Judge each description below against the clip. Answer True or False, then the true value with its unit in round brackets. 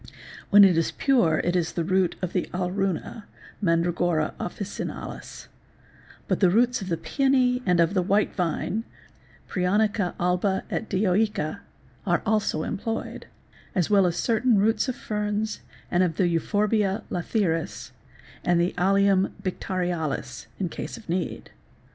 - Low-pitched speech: False (190 Hz)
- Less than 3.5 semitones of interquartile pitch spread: True (3.1 semitones)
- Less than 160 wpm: True (135 wpm)